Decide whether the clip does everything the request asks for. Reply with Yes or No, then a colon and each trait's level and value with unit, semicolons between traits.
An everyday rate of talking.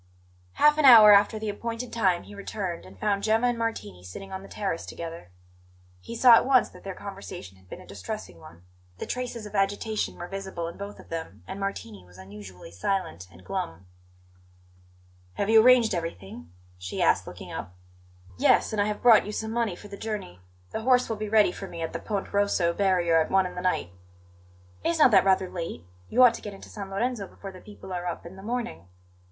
No: fast, 215 wpm